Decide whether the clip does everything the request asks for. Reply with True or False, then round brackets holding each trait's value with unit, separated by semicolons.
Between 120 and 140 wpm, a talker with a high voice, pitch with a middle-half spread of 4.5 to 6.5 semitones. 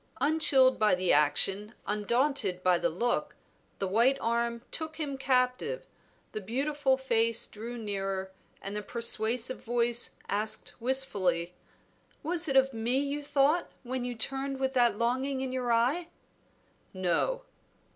False (135 wpm; 240 Hz; 4.1 semitones)